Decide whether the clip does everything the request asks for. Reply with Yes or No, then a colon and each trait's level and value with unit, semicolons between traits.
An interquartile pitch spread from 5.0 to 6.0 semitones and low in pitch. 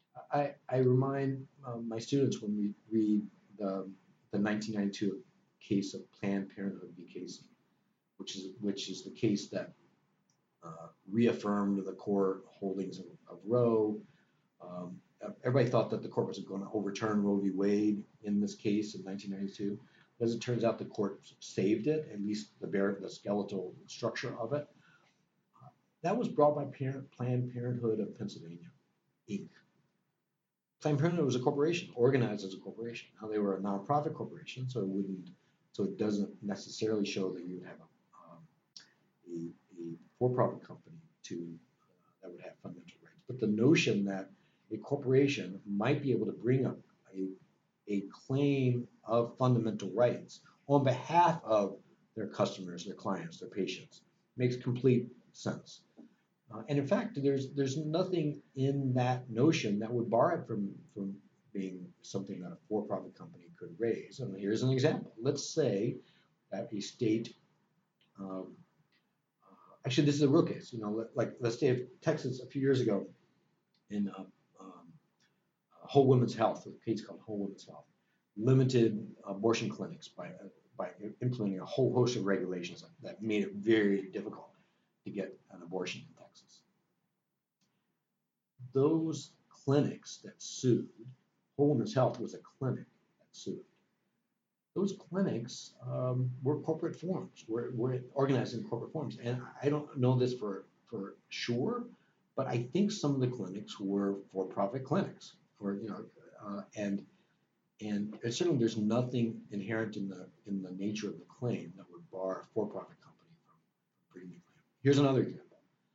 Yes: average, 5.3 semitones; low, 115 Hz